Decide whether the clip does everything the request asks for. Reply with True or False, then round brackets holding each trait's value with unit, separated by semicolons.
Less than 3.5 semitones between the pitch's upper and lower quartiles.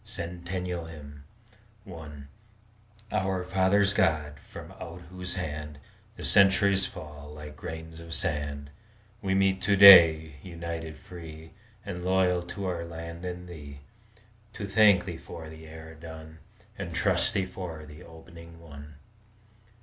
True (2.7 semitones)